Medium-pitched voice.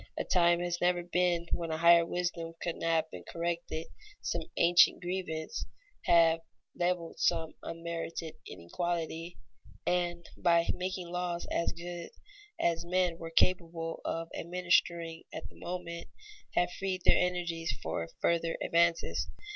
Yes: medium, 170 Hz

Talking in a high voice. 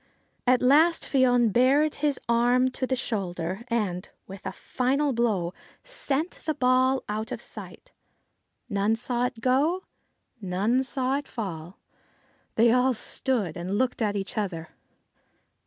Yes: high, 245 Hz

